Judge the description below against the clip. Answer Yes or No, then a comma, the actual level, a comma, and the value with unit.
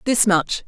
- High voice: Yes, high, 200 Hz